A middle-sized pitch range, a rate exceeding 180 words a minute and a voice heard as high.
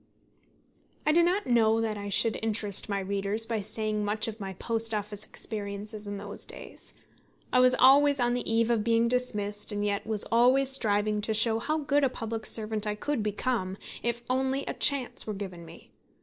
Yes: average, 3.0 semitones; average, 190 wpm; high, 220 Hz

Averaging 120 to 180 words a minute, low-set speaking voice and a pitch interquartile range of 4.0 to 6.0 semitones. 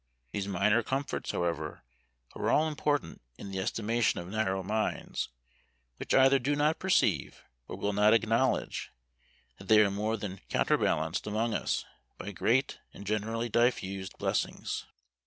No: average, 140 wpm; low, 110 Hz; average, 3.5 semitones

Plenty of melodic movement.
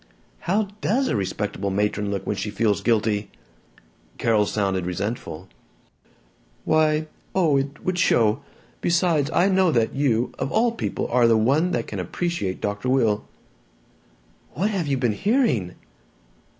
Yes: wide, 8.6 semitones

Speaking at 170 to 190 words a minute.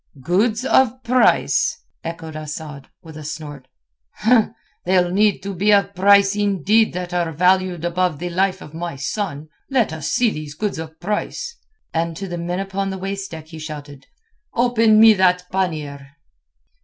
No: average, 160 wpm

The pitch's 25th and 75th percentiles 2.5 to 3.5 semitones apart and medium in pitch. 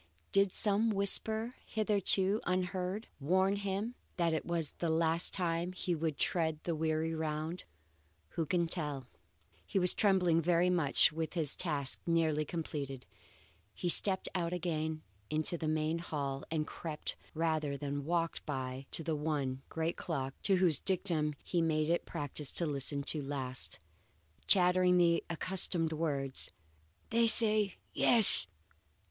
Yes: average, 3.1 semitones; medium, 165 Hz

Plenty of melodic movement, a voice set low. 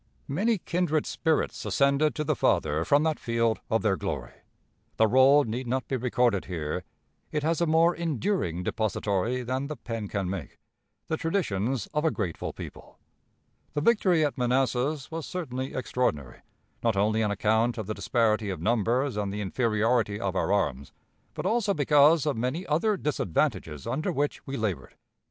Yes: wide, 6.4 semitones; low, 125 Hz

